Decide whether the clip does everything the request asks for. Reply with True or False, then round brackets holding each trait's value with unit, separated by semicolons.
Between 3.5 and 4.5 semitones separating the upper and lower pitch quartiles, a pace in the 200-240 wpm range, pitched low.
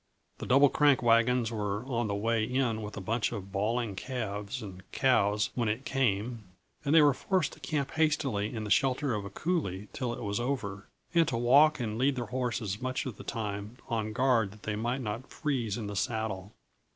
True (3.9 semitones; 205 wpm; 115 Hz)